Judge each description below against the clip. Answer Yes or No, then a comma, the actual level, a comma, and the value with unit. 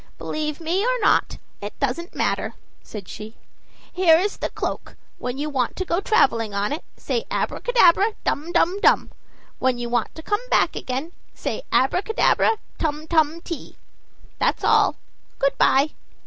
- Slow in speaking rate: No, average, 155 wpm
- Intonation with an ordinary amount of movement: No, wide, 6.1 semitones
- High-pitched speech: Yes, very high, 310 Hz